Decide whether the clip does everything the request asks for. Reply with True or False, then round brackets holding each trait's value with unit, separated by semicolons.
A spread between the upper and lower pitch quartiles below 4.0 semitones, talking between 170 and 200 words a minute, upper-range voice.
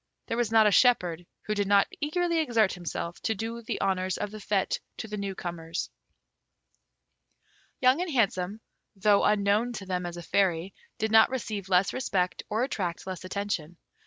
True (3.5 semitones; 175 wpm; 200 Hz)